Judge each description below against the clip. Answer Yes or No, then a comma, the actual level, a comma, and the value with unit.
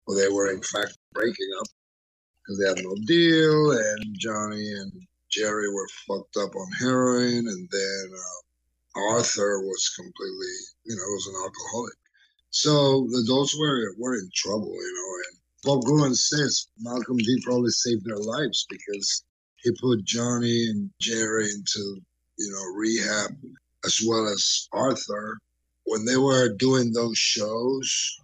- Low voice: Yes, low, 115 Hz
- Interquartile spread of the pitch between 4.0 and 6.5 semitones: Yes, average, 4.5 semitones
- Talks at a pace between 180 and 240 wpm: No, average, 150 wpm